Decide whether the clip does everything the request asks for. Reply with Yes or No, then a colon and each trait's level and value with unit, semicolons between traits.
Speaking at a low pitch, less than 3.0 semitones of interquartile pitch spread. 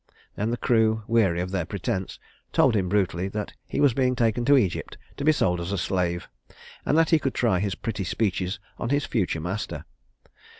No: low, 105 Hz; average, 4.7 semitones